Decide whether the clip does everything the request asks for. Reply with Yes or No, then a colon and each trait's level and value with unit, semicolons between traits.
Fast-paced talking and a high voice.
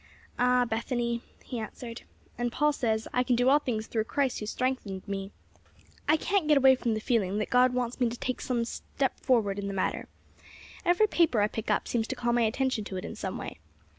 Yes: fast, 225 wpm; high, 240 Hz